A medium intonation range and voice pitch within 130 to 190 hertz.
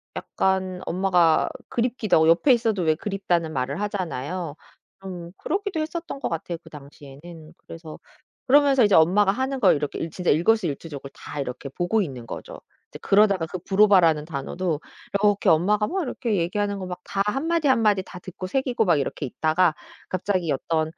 Yes: average, 4.7 semitones; medium, 185 Hz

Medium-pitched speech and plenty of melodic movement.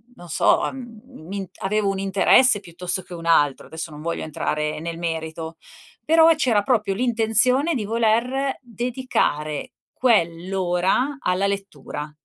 No: high, 195 Hz; wide, 6.3 semitones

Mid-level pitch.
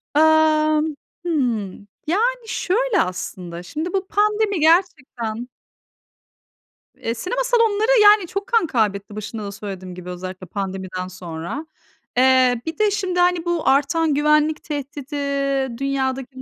No: very high, 295 Hz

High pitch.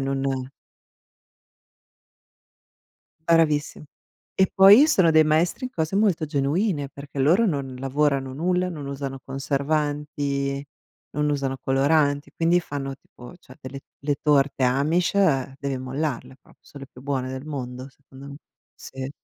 No: medium, 140 Hz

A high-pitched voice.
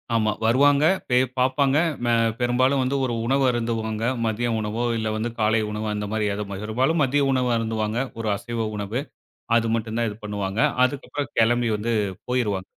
No: low, 115 Hz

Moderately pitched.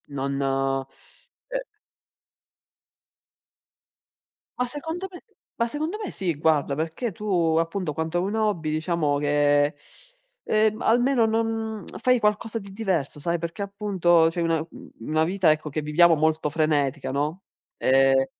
Yes: medium, 165 Hz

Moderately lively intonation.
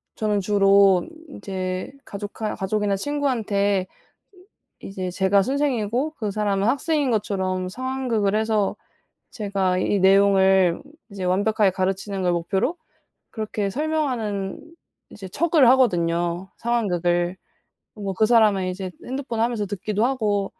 Yes: average, 3.1 semitones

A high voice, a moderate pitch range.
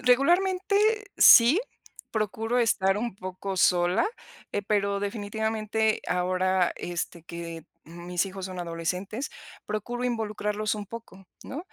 Yes: high, 205 Hz; average, 3.6 semitones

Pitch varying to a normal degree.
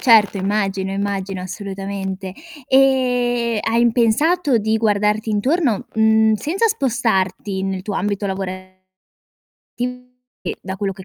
Yes: average, 3.5 semitones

